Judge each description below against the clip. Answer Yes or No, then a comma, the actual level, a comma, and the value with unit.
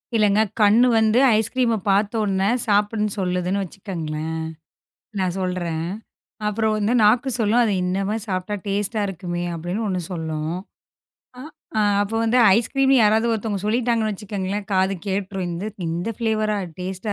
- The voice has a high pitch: Yes, high, 205 Hz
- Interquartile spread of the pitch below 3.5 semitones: Yes, average, 3.0 semitones